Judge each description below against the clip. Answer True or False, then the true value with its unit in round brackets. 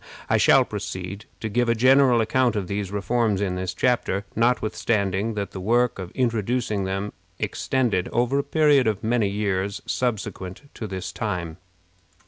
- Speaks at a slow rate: False (155 wpm)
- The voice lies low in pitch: True (110 Hz)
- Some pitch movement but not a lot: True (4.0 semitones)